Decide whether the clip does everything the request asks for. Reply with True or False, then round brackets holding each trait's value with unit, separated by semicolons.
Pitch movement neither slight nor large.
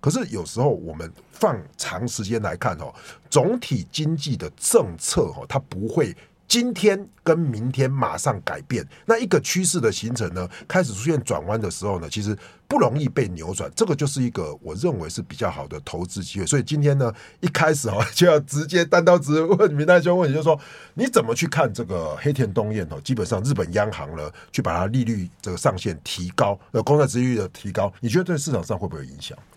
False (7.0 semitones)